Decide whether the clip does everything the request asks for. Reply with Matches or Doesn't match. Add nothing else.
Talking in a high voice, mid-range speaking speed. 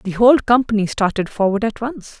Matches